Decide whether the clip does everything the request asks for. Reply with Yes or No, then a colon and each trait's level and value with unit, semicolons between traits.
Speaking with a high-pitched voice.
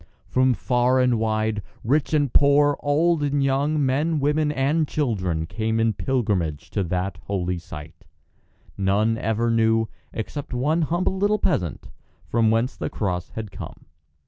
No: low, 120 Hz